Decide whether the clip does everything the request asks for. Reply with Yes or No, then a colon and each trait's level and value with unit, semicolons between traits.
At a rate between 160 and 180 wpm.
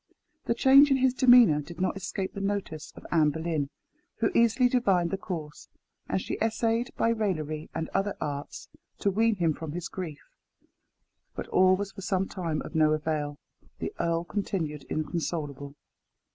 Yes: average, 165 wpm